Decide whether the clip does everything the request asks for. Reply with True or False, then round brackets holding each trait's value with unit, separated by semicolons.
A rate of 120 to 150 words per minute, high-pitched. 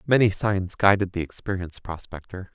False (140 wpm; 95 Hz)